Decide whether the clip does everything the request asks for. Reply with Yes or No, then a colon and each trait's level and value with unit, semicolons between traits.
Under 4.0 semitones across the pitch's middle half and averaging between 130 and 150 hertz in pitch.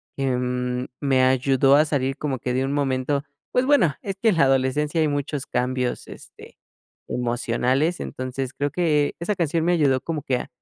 Yes: average, 2.9 semitones; low, 135 Hz